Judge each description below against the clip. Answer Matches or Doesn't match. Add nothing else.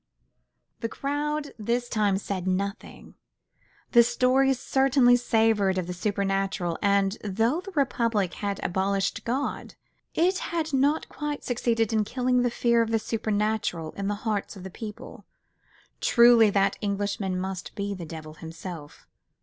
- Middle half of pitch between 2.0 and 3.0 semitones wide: Doesn't match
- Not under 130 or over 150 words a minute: Matches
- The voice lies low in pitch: Doesn't match